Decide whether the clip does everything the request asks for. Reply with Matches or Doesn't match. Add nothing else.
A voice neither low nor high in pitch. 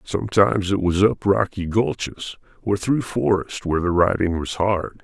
Doesn't match